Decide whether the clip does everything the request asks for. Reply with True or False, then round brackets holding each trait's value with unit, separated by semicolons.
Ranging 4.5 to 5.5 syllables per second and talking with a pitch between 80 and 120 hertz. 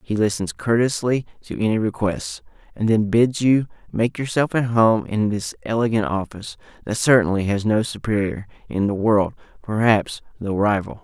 True (4.9 syllables/s; 110 Hz)